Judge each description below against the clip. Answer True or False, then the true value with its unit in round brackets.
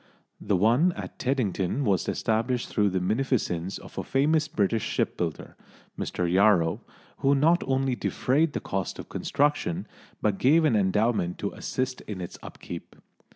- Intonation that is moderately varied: False (6.0 semitones)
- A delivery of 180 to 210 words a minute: False (150 wpm)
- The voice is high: False (110 Hz)